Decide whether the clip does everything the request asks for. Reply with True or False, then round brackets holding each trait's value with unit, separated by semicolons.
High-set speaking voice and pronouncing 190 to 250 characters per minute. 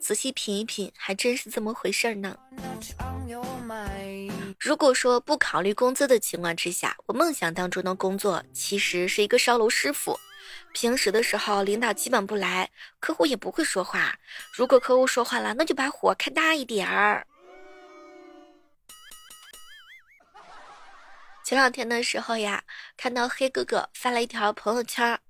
True (235 Hz; 230 characters per minute)